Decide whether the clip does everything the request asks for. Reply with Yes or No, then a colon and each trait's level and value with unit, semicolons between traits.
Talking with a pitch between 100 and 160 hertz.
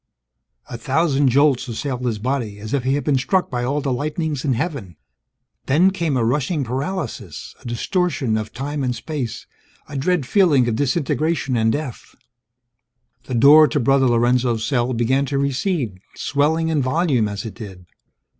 Yes: low, 135 Hz